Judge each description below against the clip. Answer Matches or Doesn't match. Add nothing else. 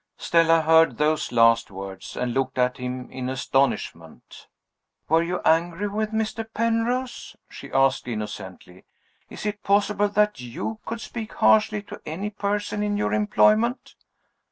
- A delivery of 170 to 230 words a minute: Doesn't match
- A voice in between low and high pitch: Matches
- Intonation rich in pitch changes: Matches